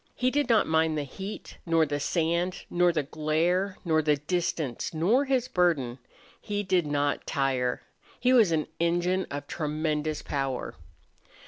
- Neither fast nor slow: Yes, average, 150 wpm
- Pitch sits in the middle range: Yes, medium, 160 Hz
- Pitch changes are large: No, average, 3.8 semitones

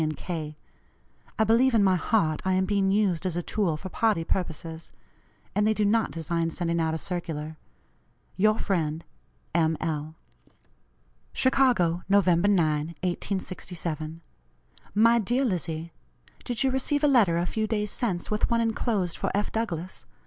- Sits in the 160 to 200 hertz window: Yes, medium, 185 Hz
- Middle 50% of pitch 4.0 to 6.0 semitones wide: Yes, average, 4.7 semitones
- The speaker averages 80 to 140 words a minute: No, average, 155 wpm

